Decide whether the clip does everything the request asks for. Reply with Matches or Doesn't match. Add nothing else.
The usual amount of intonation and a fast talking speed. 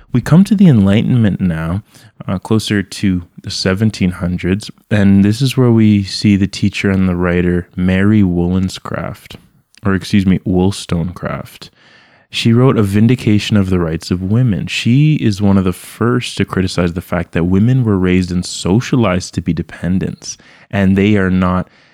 Doesn't match